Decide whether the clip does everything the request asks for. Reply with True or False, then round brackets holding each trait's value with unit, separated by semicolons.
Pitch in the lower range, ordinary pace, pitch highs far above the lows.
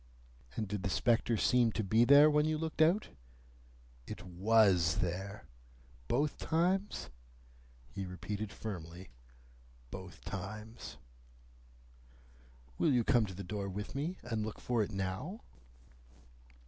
False (110 Hz; 125 wpm; 6.3 semitones)